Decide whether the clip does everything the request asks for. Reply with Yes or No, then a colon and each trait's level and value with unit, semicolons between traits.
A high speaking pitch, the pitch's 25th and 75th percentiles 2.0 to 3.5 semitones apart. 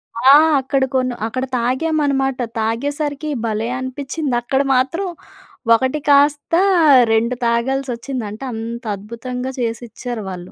Yes: very high, 255 Hz; average, 3.0 semitones